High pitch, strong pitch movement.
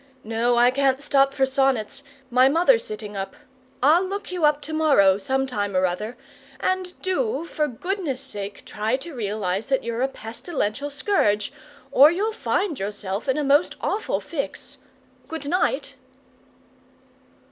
Yes: very high, 270 Hz; wide, 6.8 semitones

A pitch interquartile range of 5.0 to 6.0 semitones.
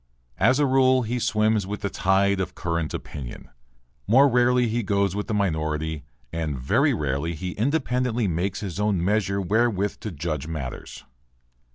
Yes: wide, 5.6 semitones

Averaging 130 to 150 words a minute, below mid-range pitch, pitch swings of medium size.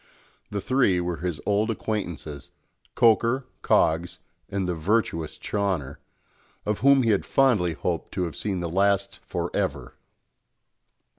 Yes: slow, 135 wpm; low, 100 Hz; average, 3.9 semitones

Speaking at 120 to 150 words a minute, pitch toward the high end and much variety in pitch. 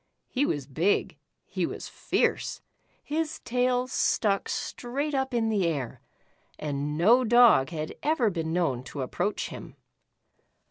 Yes: average, 140 wpm; high, 210 Hz; wide, 8.5 semitones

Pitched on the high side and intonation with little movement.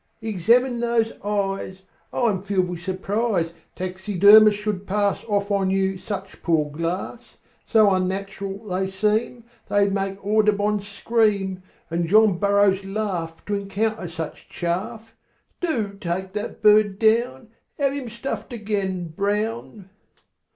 Yes: high, 200 Hz; narrow, 2.3 semitones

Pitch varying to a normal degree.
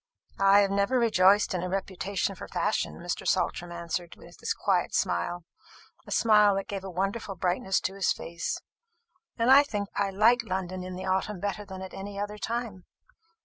No: narrow, 2.0 semitones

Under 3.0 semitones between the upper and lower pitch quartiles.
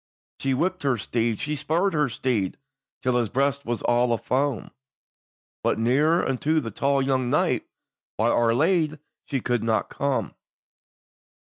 No: average, 3.8 semitones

